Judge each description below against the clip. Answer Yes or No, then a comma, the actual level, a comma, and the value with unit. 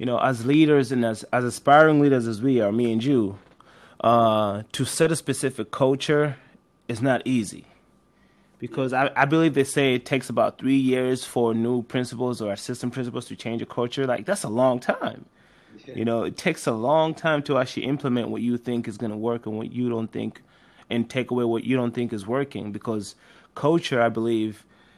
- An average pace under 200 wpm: No, fast, 205 wpm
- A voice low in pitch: Yes, low, 125 Hz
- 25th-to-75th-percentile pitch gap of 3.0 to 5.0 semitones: No, narrow, 2.6 semitones